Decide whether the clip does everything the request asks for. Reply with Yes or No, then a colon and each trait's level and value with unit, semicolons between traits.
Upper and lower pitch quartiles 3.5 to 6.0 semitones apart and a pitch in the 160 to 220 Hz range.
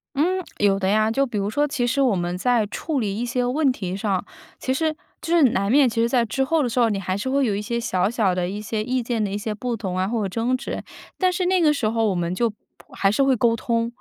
No: average, 4.5 semitones; high, 230 Hz